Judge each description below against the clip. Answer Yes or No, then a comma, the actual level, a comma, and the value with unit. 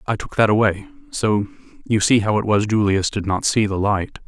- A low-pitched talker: Yes, low, 105 Hz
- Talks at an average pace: No, fast, 225 wpm